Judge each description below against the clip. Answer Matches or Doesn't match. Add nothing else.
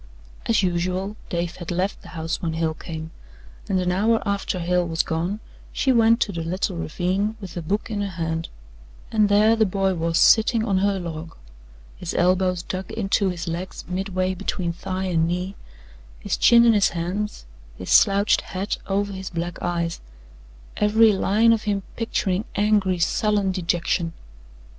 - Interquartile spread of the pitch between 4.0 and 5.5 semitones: Doesn't match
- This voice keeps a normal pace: Matches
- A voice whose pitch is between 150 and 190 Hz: Matches